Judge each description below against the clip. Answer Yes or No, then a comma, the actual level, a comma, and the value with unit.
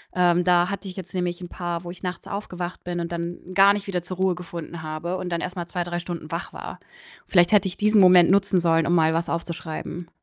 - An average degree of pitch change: No, narrow, 1.5 semitones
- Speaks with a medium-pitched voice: Yes, medium, 175 Hz